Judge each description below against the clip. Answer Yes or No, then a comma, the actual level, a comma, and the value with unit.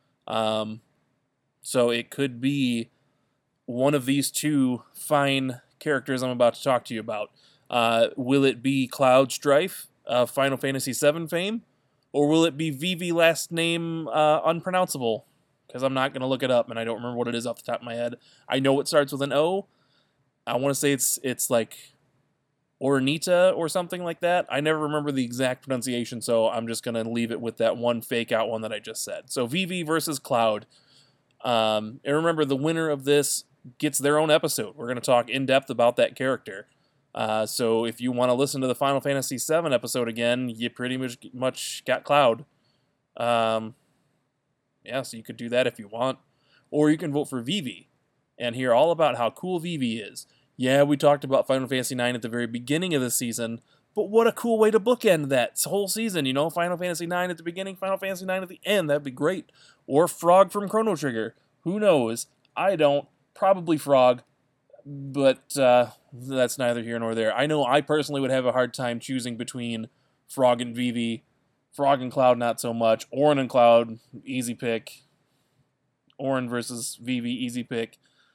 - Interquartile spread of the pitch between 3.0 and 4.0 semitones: Yes, average, 3.7 semitones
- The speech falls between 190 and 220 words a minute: Yes, average, 200 wpm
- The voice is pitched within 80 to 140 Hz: Yes, low, 135 Hz